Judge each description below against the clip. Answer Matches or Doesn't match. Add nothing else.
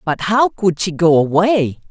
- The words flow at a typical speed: Matches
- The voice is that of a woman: Matches